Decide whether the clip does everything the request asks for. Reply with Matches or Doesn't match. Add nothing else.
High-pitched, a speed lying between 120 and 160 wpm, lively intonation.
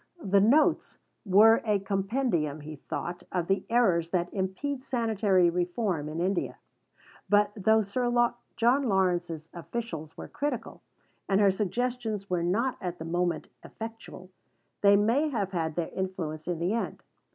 Doesn't match